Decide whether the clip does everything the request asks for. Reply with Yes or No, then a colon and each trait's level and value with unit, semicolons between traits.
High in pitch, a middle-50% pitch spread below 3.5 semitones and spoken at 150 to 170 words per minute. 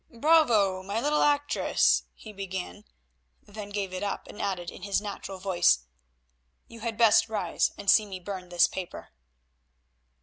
Yes: high, 200 Hz; average, 2.8 semitones; average, 155 wpm